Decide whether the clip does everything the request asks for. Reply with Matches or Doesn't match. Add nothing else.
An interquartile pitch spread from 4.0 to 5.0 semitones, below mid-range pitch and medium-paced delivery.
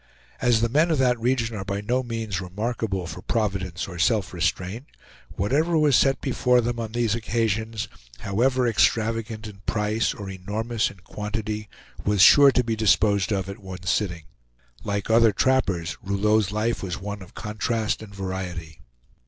Doesn't match